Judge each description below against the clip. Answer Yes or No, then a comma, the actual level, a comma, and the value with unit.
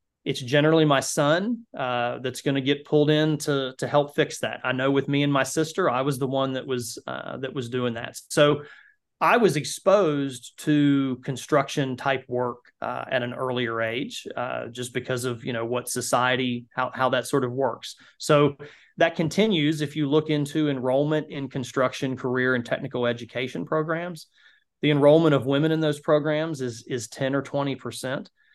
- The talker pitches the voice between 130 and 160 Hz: Yes, medium, 140 Hz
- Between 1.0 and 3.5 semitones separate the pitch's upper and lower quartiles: Yes, average, 2.9 semitones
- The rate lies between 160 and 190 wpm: Yes, average, 185 wpm